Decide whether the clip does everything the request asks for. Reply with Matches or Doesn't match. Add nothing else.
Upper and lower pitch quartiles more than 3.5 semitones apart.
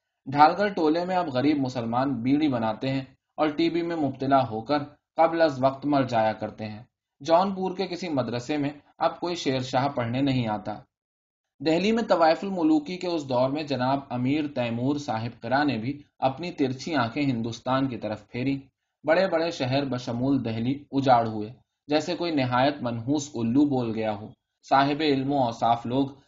Matches